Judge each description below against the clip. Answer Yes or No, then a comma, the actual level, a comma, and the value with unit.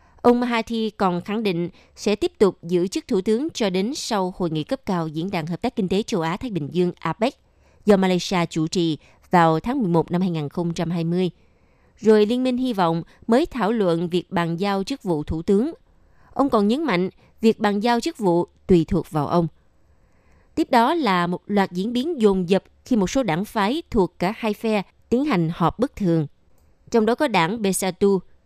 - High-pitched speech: Yes, high, 195 Hz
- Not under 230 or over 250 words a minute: No, average, 200 wpm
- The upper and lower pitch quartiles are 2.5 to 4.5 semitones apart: No, average, 4.9 semitones